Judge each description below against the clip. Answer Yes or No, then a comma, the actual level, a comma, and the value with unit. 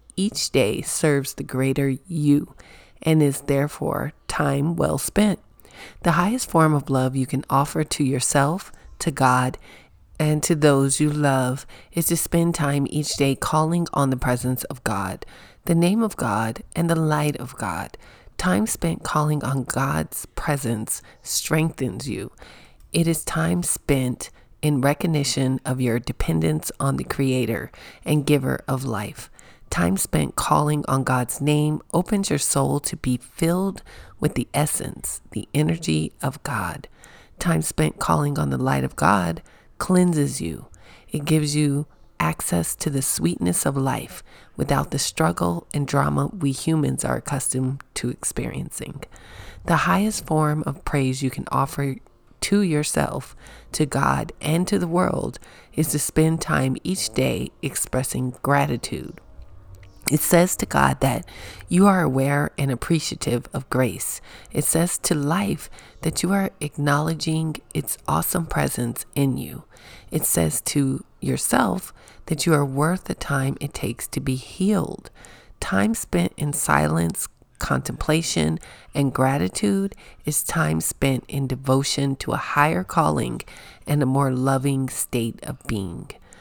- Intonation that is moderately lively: Yes, average, 3.6 semitones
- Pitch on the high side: No, medium, 140 Hz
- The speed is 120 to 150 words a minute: Yes, average, 145 wpm